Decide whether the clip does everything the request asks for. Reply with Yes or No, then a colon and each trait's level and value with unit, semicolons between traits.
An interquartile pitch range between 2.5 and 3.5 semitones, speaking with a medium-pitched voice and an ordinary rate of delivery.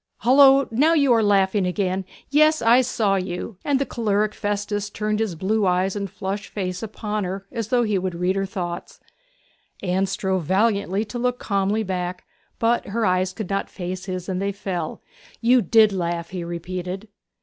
No: average, 3.2 semitones; high, 200 Hz; average, 180 wpm